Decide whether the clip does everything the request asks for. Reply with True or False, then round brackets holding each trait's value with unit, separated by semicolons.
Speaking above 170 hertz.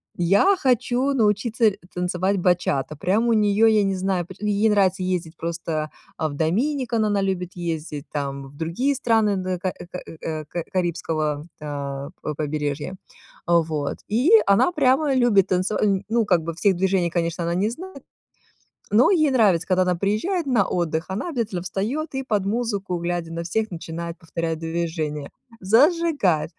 True (185 Hz)